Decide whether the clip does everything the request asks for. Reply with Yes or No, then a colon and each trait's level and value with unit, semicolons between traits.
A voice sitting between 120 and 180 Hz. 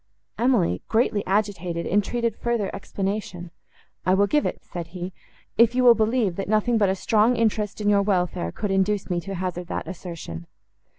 No: high, 200 Hz